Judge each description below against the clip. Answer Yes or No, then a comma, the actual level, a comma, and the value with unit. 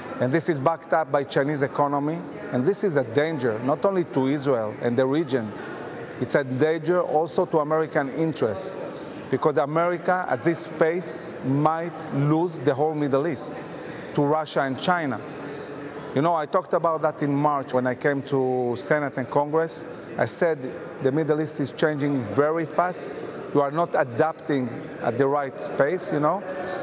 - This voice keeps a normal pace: Yes, average, 170 wpm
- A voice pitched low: No, medium, 150 Hz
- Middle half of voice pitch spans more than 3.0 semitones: No, average, 2.7 semitones